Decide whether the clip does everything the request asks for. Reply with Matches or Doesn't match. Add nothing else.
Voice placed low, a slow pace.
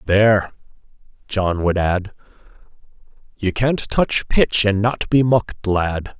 Matches